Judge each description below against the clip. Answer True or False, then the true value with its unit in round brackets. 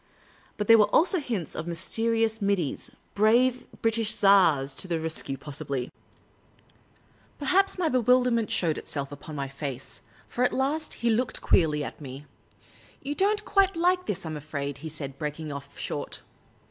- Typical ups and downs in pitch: False (9.0 semitones)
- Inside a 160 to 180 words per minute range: True (170 wpm)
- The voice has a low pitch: False (195 Hz)